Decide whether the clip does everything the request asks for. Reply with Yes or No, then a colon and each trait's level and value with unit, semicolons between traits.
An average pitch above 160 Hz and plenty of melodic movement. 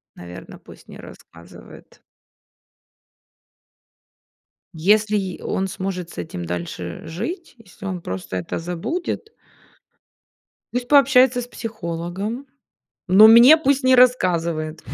Yes: high, 190 Hz; wide, 7.3 semitones